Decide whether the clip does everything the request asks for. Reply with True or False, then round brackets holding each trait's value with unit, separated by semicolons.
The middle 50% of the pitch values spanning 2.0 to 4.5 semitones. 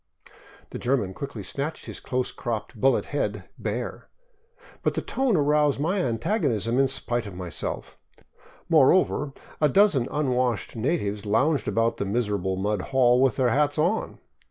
False (5.2 semitones)